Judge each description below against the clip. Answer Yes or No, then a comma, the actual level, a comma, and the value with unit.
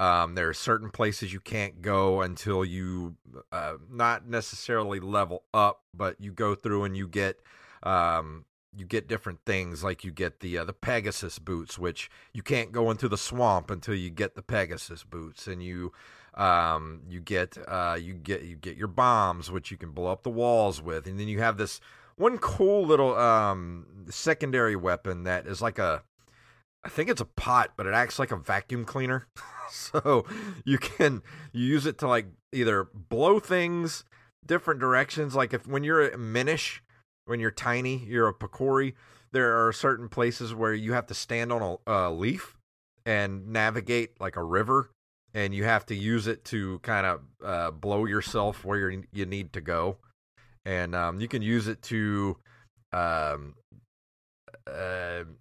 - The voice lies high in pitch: No, low, 105 Hz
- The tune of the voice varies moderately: Yes, average, 4.3 semitones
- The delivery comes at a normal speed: Yes, average, 180 wpm